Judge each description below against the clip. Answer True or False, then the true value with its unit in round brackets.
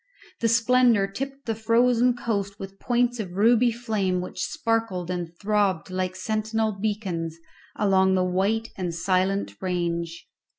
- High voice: True (200 Hz)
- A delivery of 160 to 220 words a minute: False (135 wpm)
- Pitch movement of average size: True (3.7 semitones)